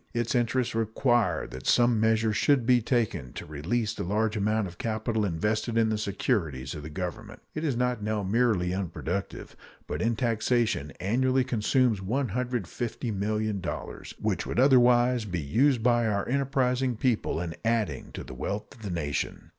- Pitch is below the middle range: Yes, low, 110 Hz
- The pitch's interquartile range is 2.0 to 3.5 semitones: No, average, 3.9 semitones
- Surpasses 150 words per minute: Yes, average, 160 wpm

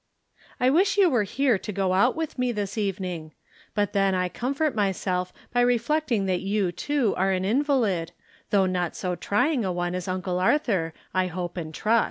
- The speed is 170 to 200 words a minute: Yes, average, 195 wpm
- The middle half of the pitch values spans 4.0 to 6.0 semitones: Yes, average, 5.2 semitones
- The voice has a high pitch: Yes, high, 195 Hz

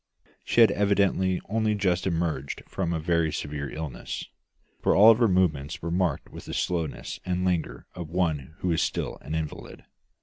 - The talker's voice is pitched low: Yes, very low, 85 Hz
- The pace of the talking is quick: No, average, 170 wpm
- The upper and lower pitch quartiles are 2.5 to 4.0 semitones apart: Yes, average, 3.0 semitones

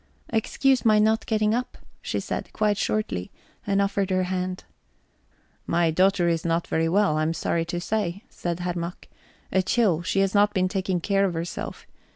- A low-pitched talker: No, medium, 185 Hz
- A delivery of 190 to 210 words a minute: No, average, 180 wpm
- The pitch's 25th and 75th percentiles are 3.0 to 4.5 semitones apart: Yes, average, 3.3 semitones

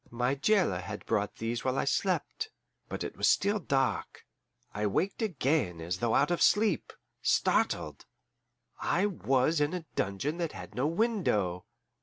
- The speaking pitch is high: No, low, 135 Hz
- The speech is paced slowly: No, average, 155 wpm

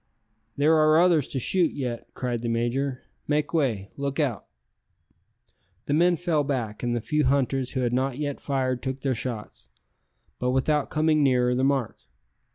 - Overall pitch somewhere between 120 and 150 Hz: Yes, low, 135 Hz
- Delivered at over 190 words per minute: No, average, 165 wpm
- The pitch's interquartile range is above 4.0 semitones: No, average, 3.1 semitones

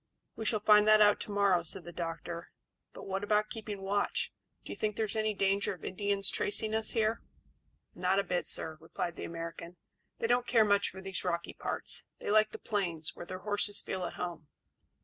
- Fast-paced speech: Yes, fast, 210 wpm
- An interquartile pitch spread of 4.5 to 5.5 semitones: No, average, 3.1 semitones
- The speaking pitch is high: Yes, high, 200 Hz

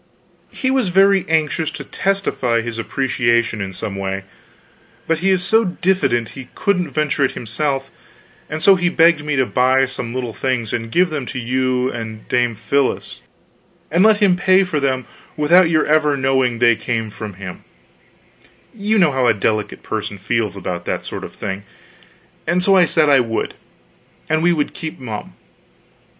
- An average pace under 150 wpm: No, average, 175 wpm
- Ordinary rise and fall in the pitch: No, wide, 6.7 semitones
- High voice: No, low, 135 Hz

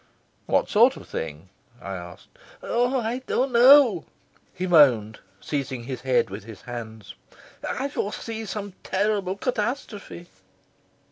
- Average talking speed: No, slow, 125 wpm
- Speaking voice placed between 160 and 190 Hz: Yes, medium, 185 Hz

